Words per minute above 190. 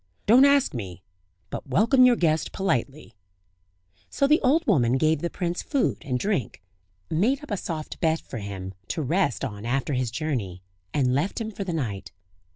No: average, 175 wpm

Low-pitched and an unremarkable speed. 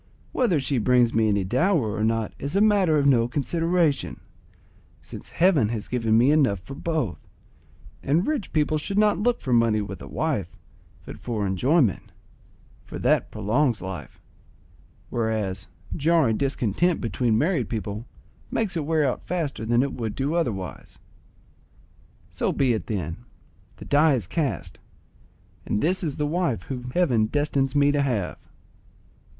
Yes: low, 130 Hz; average, 155 wpm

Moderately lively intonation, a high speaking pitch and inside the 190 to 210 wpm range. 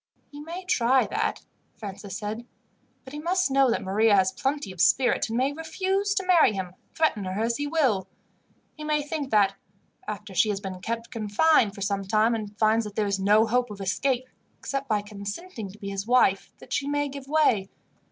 No: wide, 6.2 semitones; high, 230 Hz; average, 200 wpm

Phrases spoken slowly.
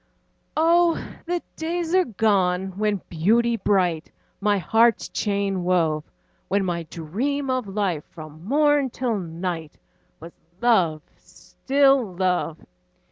Yes: slow, 115 wpm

